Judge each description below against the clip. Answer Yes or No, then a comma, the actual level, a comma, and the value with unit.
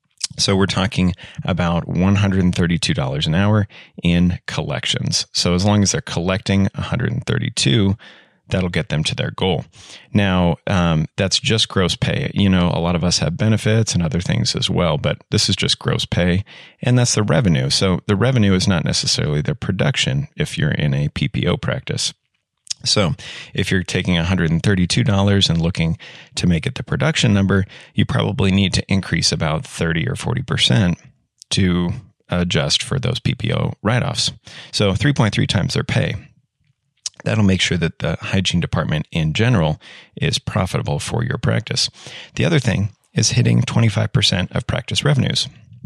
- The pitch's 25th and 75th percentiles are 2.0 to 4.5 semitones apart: Yes, average, 3.9 semitones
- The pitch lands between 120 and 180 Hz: No, low, 100 Hz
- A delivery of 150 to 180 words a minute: Yes, average, 160 wpm